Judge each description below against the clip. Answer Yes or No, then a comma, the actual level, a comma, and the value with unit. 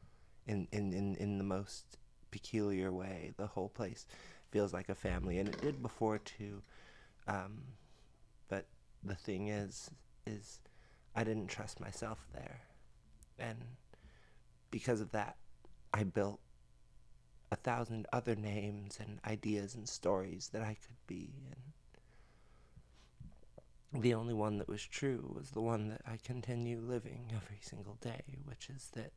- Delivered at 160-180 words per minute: No, average, 140 wpm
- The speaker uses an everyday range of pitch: Yes, average, 3.1 semitones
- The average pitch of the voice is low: Yes, low, 105 Hz